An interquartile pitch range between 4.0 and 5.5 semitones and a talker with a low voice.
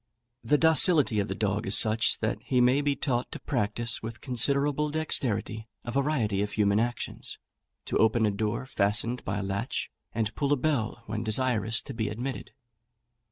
Yes: average, 4.3 semitones; low, 115 Hz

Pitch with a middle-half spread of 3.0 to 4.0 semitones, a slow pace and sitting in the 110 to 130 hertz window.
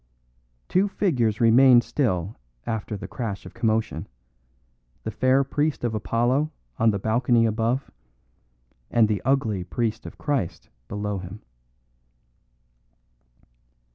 Yes: average, 3.4 semitones; slow, 110 wpm; low, 115 Hz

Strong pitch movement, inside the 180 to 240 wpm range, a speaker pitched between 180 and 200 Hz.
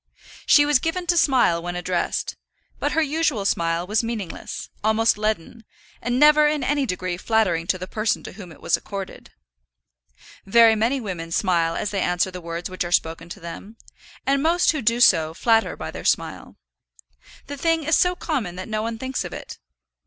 No: wide, 7.5 semitones; average, 190 wpm; high, 215 Hz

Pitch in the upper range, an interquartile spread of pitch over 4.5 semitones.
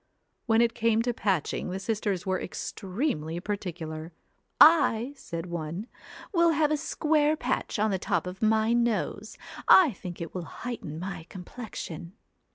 Yes: high, 205 Hz; average, 5.2 semitones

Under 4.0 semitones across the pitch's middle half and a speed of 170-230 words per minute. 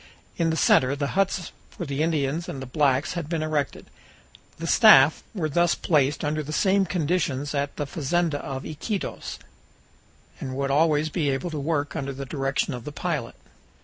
Yes: average, 3.0 semitones; average, 180 wpm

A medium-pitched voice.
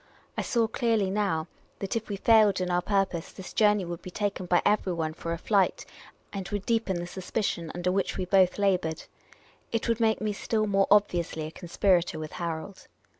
No: high, 195 Hz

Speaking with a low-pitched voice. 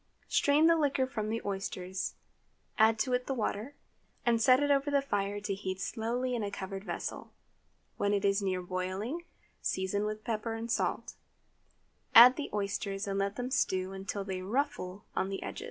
No: high, 210 Hz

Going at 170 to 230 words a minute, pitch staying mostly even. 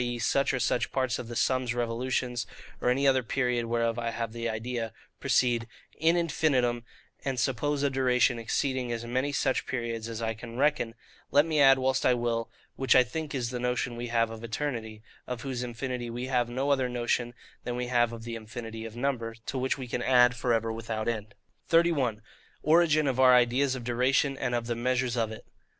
Yes: fast, 205 wpm; narrow, 2.1 semitones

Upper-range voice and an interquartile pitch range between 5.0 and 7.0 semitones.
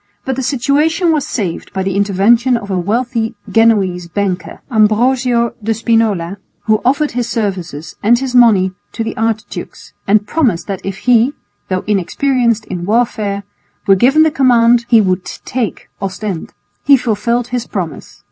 No: high, 225 Hz; average, 3.9 semitones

